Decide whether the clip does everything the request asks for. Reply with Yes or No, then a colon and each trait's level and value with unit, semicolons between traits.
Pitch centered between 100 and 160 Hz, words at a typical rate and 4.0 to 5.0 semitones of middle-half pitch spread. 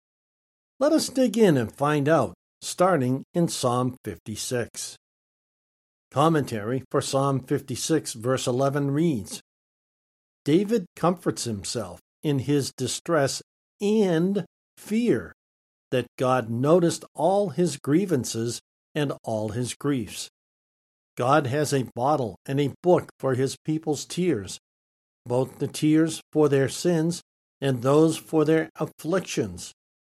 No: medium, 140 Hz; slow, 115 wpm; average, 4.5 semitones